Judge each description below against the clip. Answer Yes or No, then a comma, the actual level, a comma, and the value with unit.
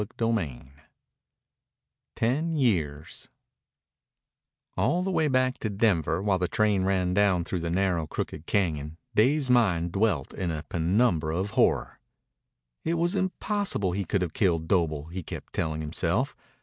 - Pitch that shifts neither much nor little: No, wide, 5.8 semitones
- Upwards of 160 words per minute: No, average, 145 wpm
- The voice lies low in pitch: Yes, very low, 95 Hz